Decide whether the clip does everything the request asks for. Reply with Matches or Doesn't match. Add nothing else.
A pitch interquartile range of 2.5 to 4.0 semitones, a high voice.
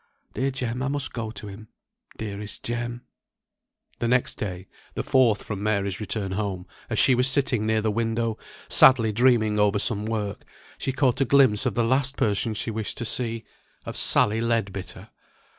Doesn't match